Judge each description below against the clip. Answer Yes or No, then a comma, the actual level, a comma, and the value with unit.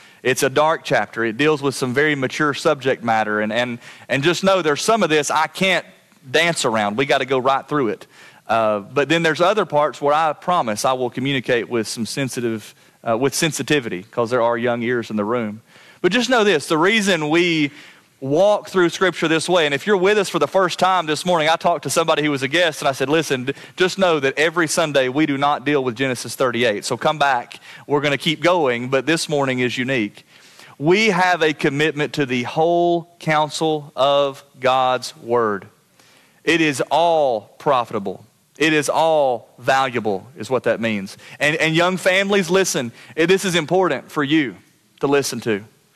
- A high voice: No, medium, 150 Hz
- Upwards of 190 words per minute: Yes, average, 200 wpm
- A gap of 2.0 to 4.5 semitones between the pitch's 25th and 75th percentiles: No, average, 5.0 semitones